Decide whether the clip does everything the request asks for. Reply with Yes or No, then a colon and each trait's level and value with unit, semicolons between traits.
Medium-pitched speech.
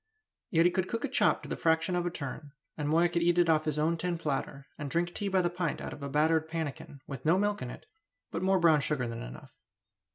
Yes: medium, 165 Hz